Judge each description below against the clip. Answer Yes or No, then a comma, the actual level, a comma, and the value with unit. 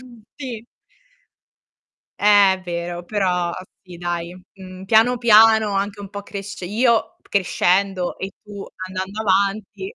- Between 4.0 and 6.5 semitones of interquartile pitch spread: No, average, 2.8 semitones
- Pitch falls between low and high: No, high, 200 Hz